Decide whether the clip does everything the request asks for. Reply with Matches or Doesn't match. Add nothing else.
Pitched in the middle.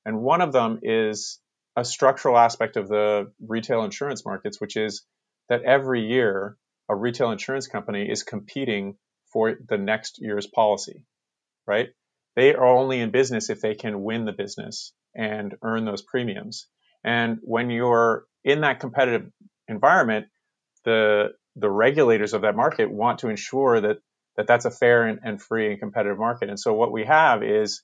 Doesn't match